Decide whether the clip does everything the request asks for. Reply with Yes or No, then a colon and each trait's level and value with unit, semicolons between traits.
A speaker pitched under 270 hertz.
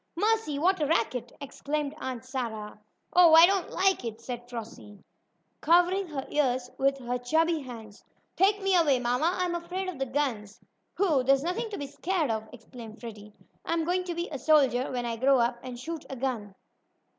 No: very high, 275 Hz